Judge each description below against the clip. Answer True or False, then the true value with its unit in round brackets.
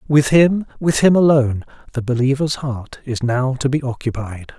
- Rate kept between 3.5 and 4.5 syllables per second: False (4.7 syllables/s)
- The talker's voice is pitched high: False (135 Hz)